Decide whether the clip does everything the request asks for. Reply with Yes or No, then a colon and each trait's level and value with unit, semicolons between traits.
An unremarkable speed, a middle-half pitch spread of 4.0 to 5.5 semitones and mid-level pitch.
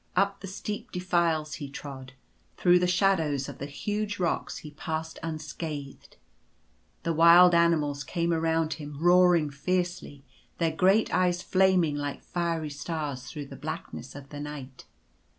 No: average, 150 wpm; average, 3.5 semitones; medium, 160 Hz